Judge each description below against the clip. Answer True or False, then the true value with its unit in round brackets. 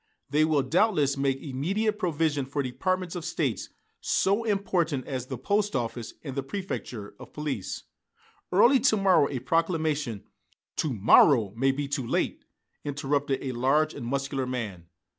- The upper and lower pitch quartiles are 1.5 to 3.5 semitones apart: False (4.9 semitones)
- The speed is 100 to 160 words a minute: True (155 wpm)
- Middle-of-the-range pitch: True (145 Hz)